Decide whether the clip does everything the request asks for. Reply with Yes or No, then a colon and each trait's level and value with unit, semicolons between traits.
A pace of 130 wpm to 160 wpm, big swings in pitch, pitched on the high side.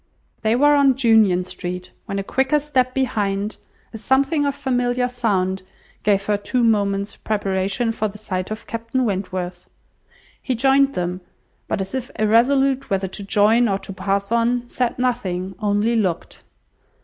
No: average, 155 wpm; average, 4.3 semitones; high, 220 Hz